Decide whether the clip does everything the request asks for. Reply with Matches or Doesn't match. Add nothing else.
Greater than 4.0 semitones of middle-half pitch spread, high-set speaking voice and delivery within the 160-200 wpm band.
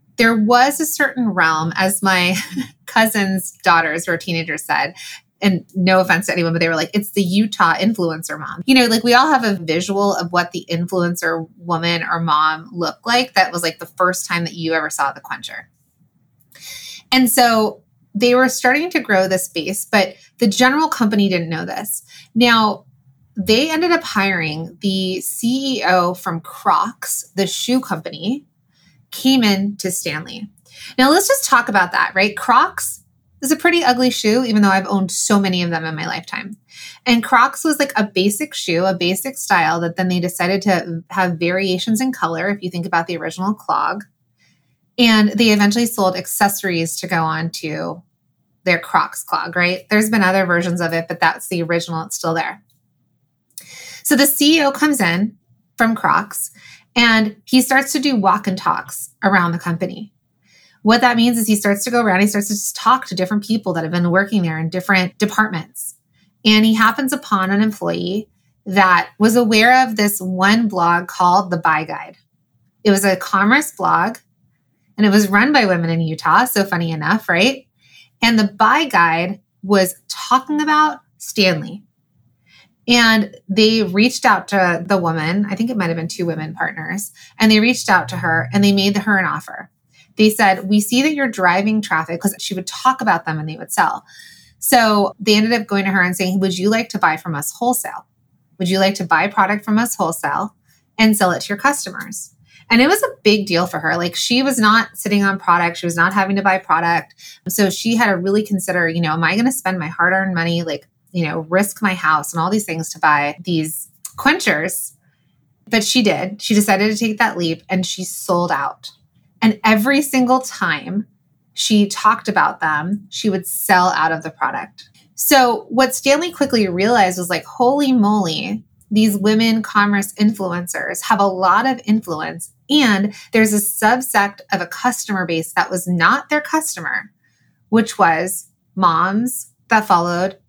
Matches